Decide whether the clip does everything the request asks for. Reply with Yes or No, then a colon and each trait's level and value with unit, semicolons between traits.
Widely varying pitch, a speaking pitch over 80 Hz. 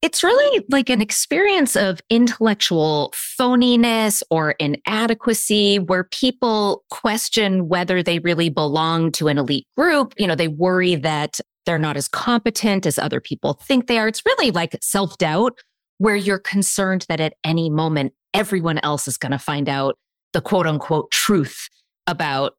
Yes: wide, 6.1 semitones; high, 190 Hz